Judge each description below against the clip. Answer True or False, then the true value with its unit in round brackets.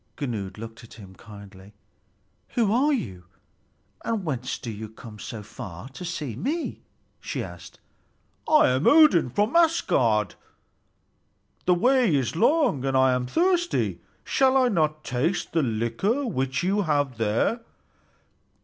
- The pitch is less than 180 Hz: True (140 Hz)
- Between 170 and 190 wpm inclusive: False (140 wpm)